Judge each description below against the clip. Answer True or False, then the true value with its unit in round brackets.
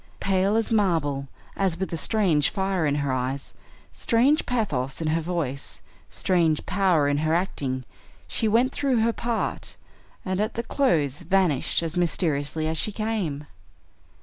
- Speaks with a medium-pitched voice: True (175 Hz)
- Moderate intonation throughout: False (6.3 semitones)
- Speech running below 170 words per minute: True (150 wpm)